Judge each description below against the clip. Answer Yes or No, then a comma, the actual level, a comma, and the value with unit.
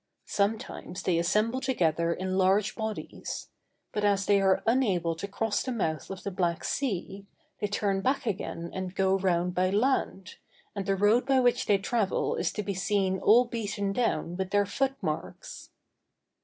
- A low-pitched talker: No, high, 200 Hz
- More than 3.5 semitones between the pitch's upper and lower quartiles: No, average, 2.8 semitones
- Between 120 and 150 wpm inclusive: No, average, 170 wpm